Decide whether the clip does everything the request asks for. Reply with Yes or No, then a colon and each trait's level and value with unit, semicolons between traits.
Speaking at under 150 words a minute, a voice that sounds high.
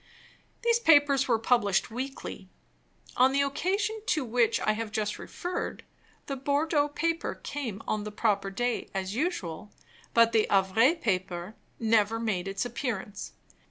Yes: average, 140 wpm; high, 230 Hz